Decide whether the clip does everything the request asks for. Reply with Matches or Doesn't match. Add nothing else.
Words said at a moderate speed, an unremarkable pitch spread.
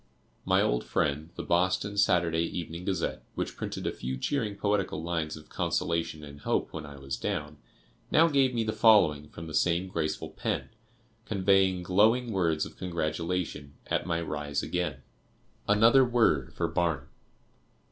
Matches